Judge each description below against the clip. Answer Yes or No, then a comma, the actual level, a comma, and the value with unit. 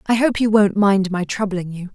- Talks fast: Yes, fast, 245 wpm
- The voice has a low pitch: No, high, 200 Hz